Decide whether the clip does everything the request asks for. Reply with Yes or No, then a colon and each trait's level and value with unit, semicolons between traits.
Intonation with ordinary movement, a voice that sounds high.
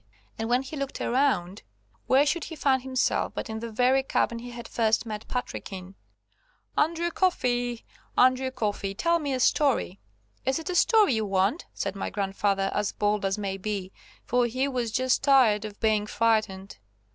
Yes: average, 4.3 semitones; high, 235 Hz